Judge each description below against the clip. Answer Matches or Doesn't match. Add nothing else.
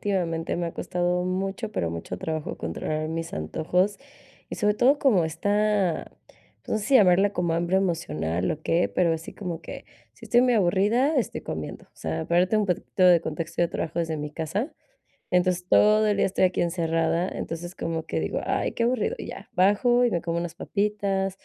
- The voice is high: Doesn't match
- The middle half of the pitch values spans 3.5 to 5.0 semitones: Matches